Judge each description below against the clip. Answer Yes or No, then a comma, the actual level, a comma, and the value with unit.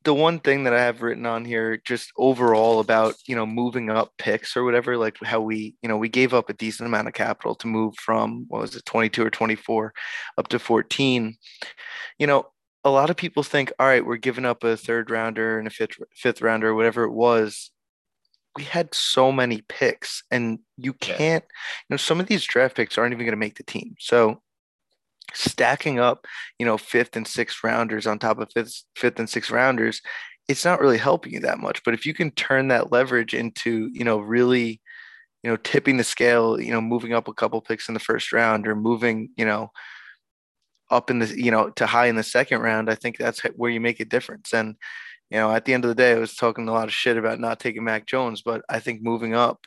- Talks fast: Yes, fast, 230 wpm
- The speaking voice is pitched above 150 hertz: No, low, 115 Hz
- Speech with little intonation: Yes, narrow, 1.8 semitones